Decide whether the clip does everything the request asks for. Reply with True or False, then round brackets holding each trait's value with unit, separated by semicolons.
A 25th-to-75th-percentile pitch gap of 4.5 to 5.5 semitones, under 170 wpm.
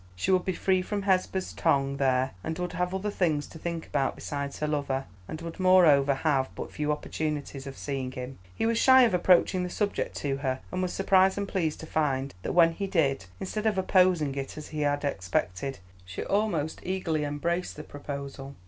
False (4.9 semitones; 200 wpm)